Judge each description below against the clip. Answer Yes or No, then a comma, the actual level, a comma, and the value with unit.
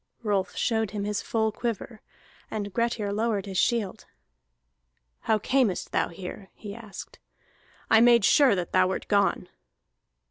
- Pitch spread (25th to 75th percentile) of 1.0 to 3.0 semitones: Yes, average, 2.7 semitones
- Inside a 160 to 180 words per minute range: No, average, 140 wpm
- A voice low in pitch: No, high, 210 Hz